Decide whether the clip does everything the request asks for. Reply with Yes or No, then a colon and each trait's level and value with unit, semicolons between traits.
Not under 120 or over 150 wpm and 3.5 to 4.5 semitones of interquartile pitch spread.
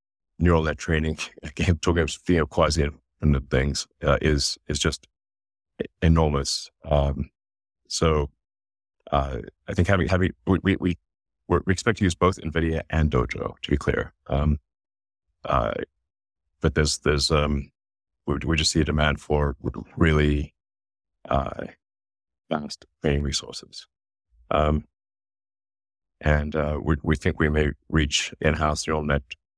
No: average, 140 wpm; narrow, 2.5 semitones